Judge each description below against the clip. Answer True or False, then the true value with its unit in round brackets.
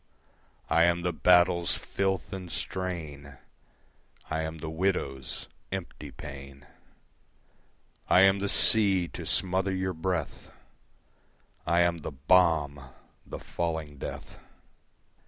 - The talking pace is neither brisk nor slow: False (110 wpm)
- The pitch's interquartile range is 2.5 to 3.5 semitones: True (3.1 semitones)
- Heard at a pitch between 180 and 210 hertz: False (85 Hz)